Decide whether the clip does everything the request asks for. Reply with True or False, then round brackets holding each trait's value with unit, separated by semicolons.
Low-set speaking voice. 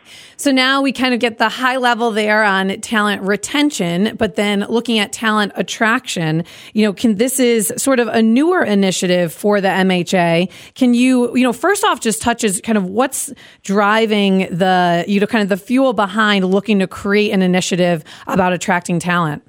False (210 Hz)